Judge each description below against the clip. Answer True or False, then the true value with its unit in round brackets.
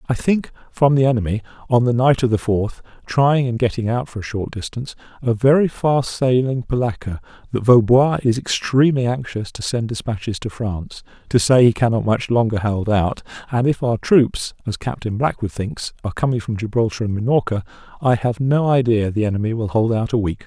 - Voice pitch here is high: False (120 Hz)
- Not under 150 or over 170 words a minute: False (195 wpm)